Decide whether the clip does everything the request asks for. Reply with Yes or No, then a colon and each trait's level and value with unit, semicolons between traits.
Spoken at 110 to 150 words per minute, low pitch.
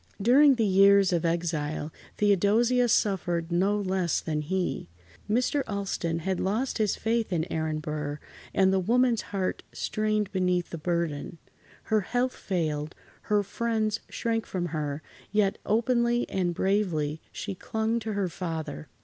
No: average, 140 wpm; high, 190 Hz